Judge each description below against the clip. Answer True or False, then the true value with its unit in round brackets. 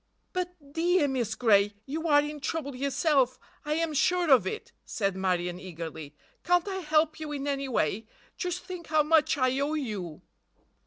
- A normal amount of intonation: False (6.8 semitones)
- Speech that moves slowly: False (165 wpm)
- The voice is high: True (285 Hz)